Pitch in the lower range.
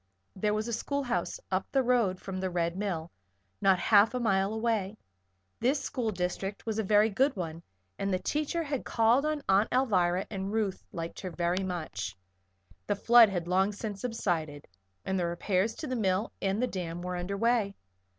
No: high, 200 Hz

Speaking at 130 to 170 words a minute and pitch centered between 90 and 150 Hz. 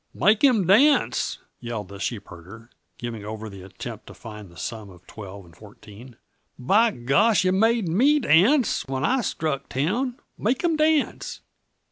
Yes: average, 155 wpm; low, 135 Hz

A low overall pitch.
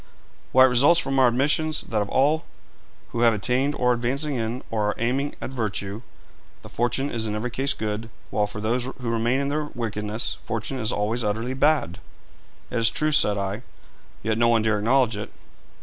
Yes: low, 120 Hz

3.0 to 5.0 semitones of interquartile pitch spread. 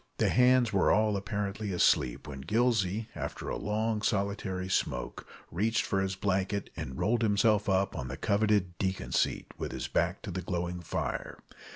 No: narrow, 2.6 semitones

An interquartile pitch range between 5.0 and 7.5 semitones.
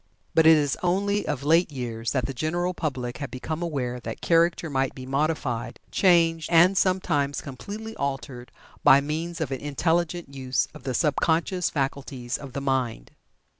No: average, 4.2 semitones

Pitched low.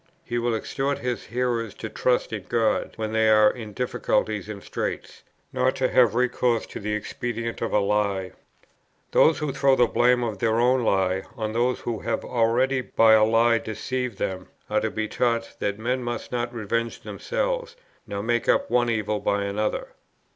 Yes: low, 115 Hz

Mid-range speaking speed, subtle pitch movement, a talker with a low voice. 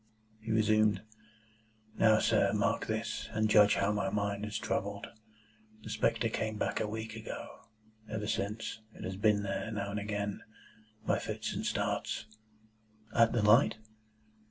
Yes: average, 150 wpm; narrow, 1.2 semitones; low, 105 Hz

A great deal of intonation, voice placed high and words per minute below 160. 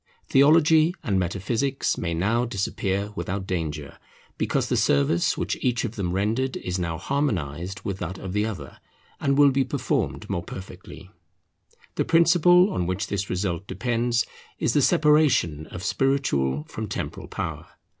No: wide, 7.2 semitones; low, 100 Hz; average, 150 wpm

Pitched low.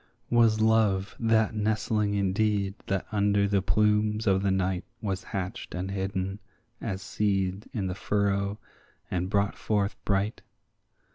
Yes: low, 100 Hz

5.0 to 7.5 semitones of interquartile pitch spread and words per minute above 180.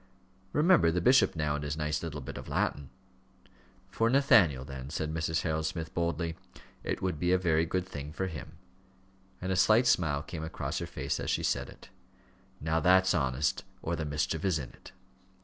No: average, 3.5 semitones; average, 190 wpm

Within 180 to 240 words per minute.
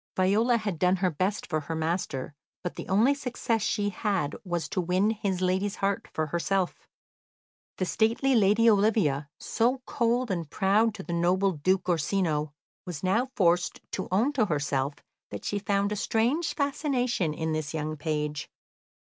No: average, 165 wpm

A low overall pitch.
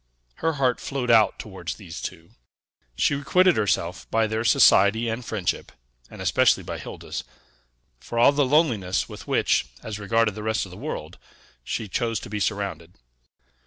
Yes: low, 110 Hz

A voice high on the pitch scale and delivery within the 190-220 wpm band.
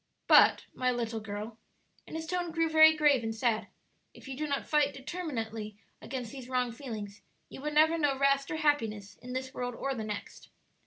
Yes: very high, 260 Hz; average, 195 wpm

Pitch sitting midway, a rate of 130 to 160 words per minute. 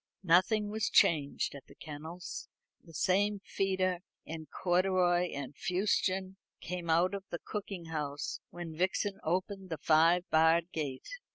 Yes: medium, 175 Hz; average, 140 wpm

